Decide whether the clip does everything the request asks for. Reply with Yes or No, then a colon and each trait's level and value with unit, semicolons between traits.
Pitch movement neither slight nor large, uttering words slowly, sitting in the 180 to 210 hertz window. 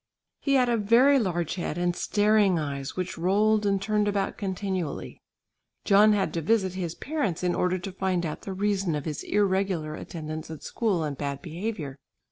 No: average, 4.0 semitones; average, 180 wpm; high, 190 Hz